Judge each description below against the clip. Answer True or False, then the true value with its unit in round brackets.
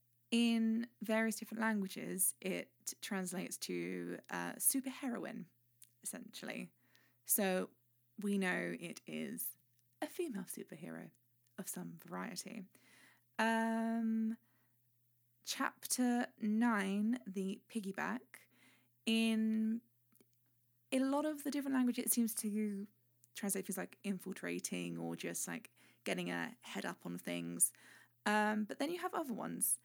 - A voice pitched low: False (195 Hz)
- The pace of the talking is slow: True (115 wpm)